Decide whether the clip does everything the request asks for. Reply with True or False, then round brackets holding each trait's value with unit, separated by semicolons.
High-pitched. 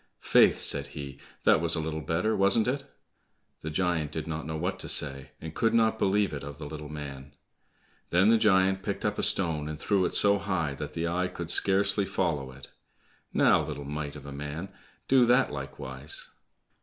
False (80 Hz)